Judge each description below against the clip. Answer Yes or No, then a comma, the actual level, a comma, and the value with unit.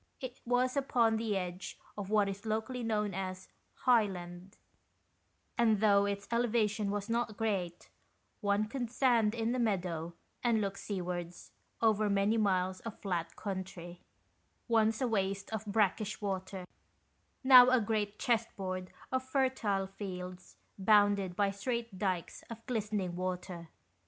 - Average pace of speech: Yes, average, 145 wpm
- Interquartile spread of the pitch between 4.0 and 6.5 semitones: No, average, 3.2 semitones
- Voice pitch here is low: No, high, 205 Hz